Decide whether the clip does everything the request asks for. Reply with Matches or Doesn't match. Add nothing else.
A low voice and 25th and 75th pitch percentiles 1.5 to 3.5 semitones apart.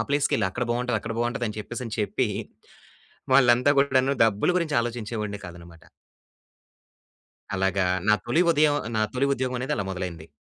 Doesn't match